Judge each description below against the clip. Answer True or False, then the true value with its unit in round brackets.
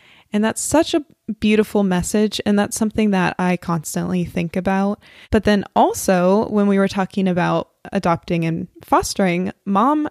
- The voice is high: True (195 Hz)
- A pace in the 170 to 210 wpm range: False (155 wpm)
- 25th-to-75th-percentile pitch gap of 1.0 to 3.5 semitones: True (3.2 semitones)